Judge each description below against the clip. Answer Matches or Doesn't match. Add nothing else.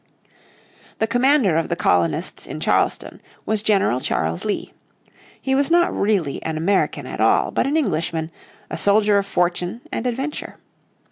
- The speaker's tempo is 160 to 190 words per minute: Doesn't match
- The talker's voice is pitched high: Matches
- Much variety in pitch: Matches